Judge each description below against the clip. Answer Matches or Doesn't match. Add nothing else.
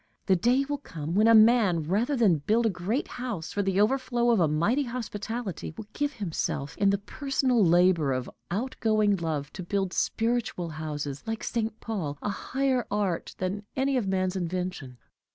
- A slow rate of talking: Doesn't match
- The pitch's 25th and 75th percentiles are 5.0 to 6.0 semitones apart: Matches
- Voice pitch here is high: Matches